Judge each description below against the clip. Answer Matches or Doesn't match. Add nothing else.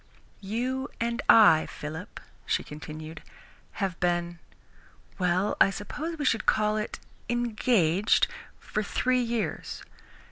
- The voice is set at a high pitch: Matches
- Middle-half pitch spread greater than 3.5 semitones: Matches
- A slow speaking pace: Matches